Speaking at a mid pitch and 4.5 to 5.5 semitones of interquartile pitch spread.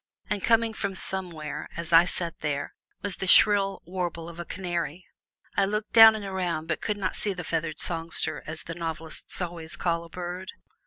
No: medium, 175 Hz; average, 2.9 semitones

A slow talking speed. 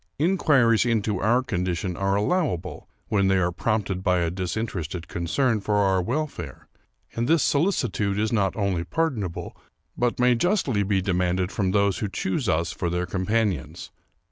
No: average, 160 wpm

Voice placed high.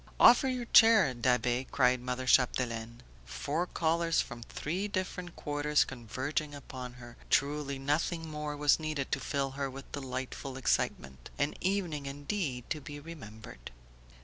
No: medium, 140 Hz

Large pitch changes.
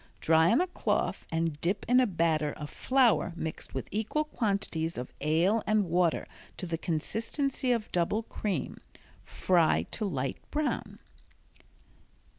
Yes: wide, 5.8 semitones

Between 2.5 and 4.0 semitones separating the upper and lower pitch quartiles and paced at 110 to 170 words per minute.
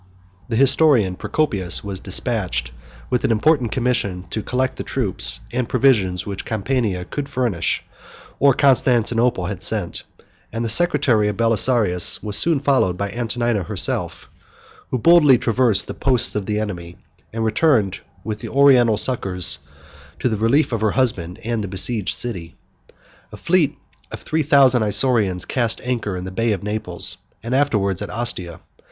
No: average, 4.6 semitones; average, 160 wpm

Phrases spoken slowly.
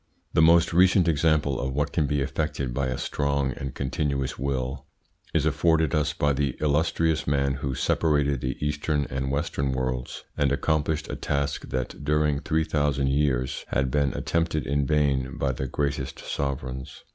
No: average, 165 wpm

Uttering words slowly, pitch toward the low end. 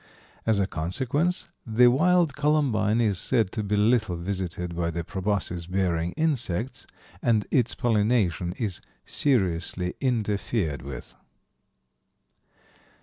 Yes: slow, 110 wpm; low, 105 Hz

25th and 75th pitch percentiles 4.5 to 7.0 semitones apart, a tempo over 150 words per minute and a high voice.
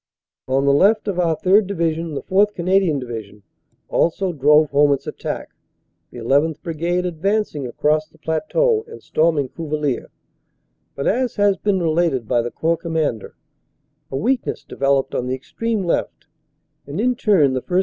No: wide, 5.6 semitones; average, 160 wpm; medium, 160 Hz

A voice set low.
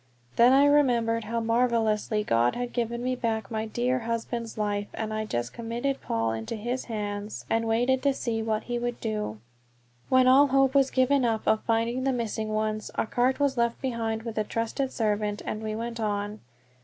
No: high, 230 Hz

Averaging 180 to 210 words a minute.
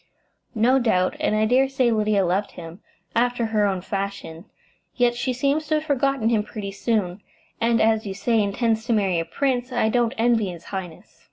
Yes: average, 190 wpm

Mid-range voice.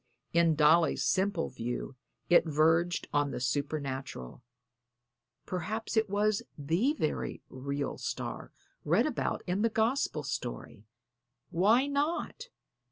Yes: medium, 165 Hz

